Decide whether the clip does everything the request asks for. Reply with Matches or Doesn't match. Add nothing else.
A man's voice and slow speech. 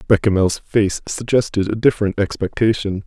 Matches